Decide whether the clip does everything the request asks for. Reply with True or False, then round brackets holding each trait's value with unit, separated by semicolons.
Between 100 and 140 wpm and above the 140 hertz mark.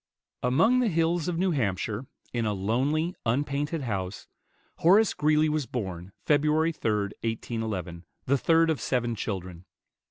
False (135 wpm; 130 Hz)